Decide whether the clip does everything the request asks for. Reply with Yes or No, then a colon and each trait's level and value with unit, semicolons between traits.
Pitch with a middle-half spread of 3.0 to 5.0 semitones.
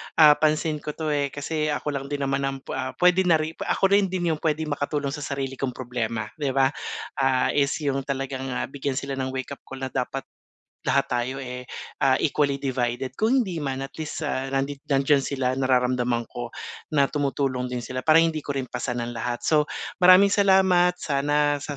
No: narrow, 2.6 semitones